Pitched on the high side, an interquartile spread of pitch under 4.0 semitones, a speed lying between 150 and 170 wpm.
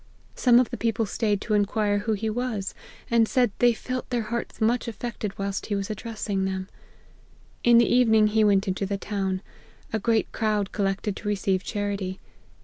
No: high, 210 Hz; average, 2.7 semitones; average, 180 wpm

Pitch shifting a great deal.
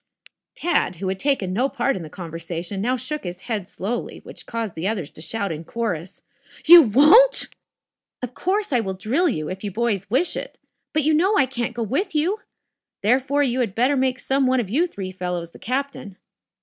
Yes: wide, 6.7 semitones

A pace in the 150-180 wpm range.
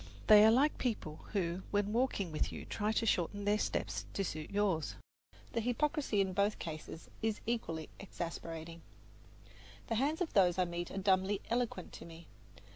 Yes: average, 170 wpm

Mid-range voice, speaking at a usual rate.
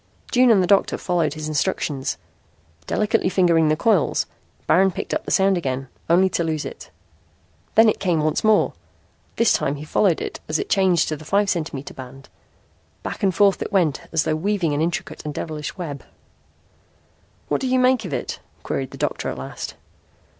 Yes: medium, 170 Hz; average, 185 wpm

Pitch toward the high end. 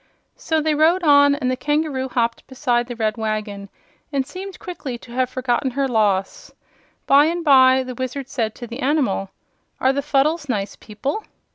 Yes: very high, 260 Hz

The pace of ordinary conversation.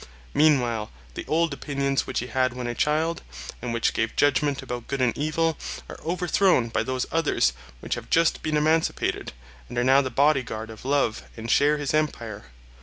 Yes: average, 185 wpm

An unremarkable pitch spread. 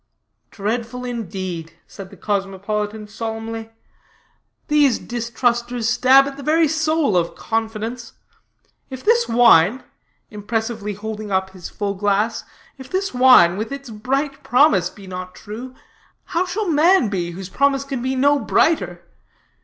Yes: average, 4.9 semitones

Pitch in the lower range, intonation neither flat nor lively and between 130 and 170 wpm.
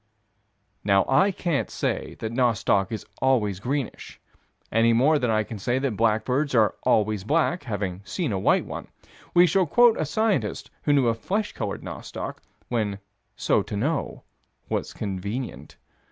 No: low, 120 Hz; wide, 5.7 semitones; average, 155 wpm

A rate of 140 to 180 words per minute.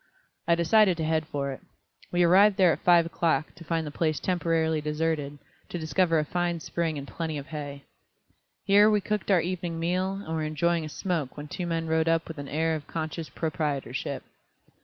No: average, 200 wpm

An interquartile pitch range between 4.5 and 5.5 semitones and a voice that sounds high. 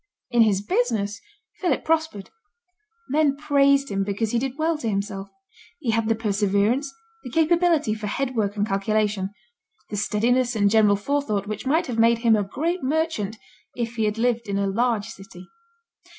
Yes: average, 5.0 semitones; high, 225 Hz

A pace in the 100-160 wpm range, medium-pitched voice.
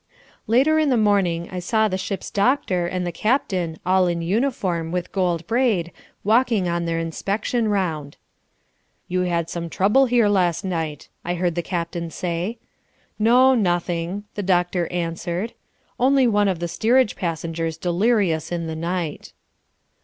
Yes: average, 150 wpm; medium, 180 Hz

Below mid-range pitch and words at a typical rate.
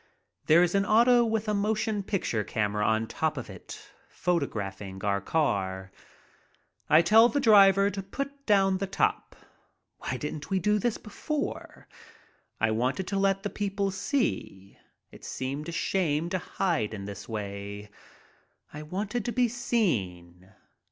No: medium, 185 Hz; average, 150 wpm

